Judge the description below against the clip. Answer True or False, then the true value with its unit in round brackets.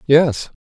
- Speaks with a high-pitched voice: False (150 Hz)